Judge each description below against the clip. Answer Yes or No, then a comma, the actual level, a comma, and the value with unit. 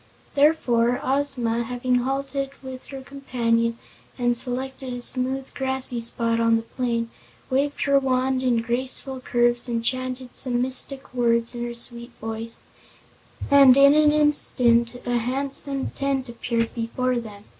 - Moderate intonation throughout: No, narrow, 2.2 semitones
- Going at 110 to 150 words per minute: Yes, average, 140 wpm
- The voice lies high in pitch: Yes, very high, 250 Hz